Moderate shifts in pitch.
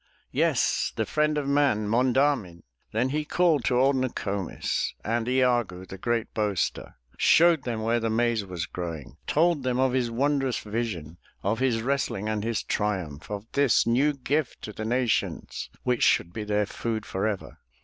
Yes: average, 4.2 semitones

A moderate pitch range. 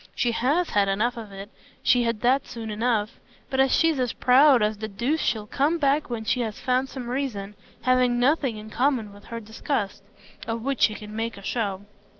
Yes: average, 3.7 semitones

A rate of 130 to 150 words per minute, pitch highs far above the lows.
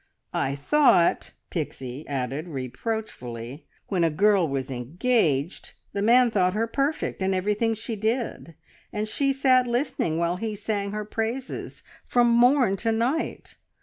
Yes: average, 140 wpm; wide, 6.8 semitones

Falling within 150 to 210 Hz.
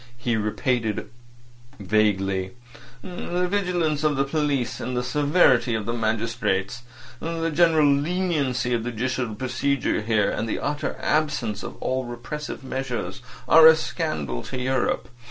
No: low, 130 Hz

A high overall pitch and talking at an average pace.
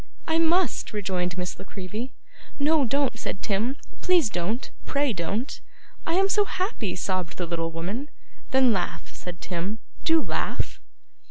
Yes: high, 220 Hz; average, 150 wpm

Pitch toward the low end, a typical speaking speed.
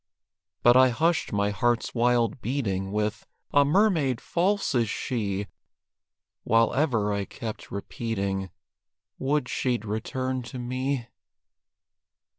No: low, 120 Hz; slow, 110 wpm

